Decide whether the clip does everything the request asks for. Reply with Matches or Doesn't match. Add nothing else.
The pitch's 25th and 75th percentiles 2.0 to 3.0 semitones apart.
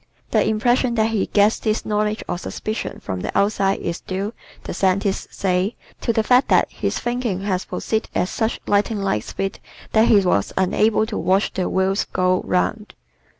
Matches